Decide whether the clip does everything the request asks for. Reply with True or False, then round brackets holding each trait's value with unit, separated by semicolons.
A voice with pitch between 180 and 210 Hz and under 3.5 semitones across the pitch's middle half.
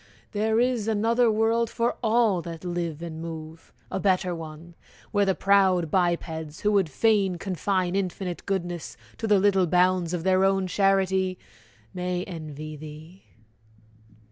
True (185 Hz; 3.0 semitones)